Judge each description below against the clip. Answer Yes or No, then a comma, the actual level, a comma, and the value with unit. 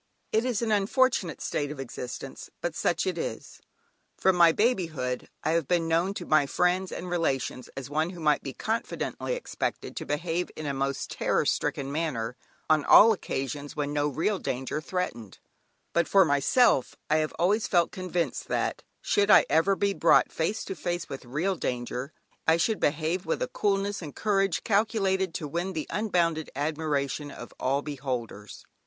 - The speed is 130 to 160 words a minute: No, average, 175 wpm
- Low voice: No, medium, 165 Hz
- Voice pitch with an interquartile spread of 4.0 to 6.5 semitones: Yes, average, 4.9 semitones